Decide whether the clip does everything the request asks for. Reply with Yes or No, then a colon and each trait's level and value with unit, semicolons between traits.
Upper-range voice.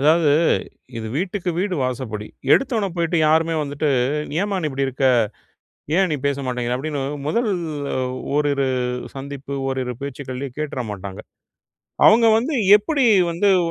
No: medium, 145 Hz